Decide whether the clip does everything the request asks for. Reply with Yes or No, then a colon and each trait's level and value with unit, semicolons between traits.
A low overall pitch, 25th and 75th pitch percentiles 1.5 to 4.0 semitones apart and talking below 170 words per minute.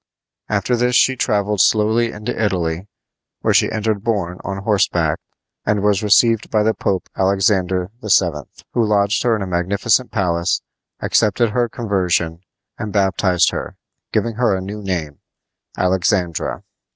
Yes: low, 100 Hz; average, 3.0 semitones; average, 140 wpm